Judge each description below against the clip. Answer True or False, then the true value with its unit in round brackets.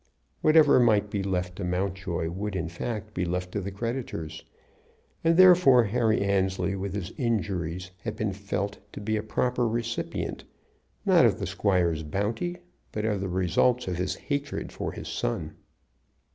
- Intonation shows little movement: False (4.2 semitones)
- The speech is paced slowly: False (160 wpm)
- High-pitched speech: False (100 Hz)